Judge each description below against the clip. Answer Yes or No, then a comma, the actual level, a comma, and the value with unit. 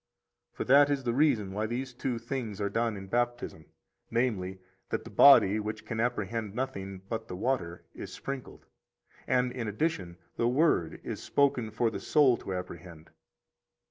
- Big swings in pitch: No, average, 4.7 semitones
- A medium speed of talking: Yes, average, 170 wpm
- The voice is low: Yes, low, 115 Hz